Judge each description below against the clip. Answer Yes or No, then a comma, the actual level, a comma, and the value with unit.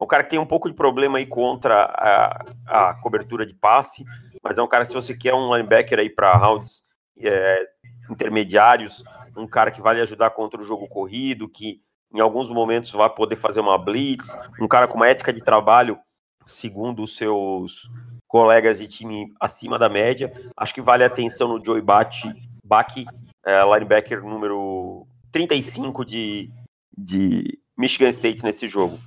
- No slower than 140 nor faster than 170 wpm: Yes, average, 165 wpm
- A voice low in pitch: Yes, low, 115 Hz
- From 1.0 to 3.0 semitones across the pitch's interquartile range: Yes, narrow, 2.6 semitones